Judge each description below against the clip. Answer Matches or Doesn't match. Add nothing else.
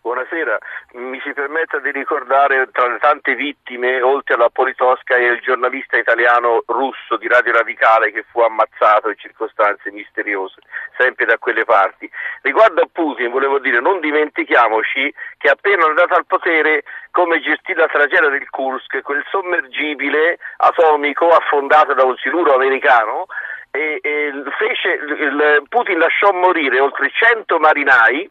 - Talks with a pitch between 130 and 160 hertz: Matches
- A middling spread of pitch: Matches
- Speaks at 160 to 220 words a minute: Doesn't match